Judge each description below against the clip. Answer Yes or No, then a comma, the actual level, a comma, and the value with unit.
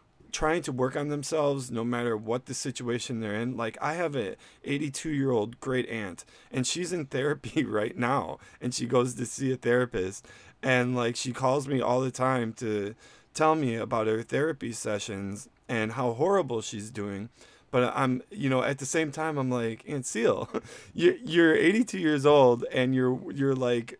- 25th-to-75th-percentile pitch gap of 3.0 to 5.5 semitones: Yes, average, 3.3 semitones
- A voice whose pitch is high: No, low, 125 Hz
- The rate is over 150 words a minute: Yes, average, 185 wpm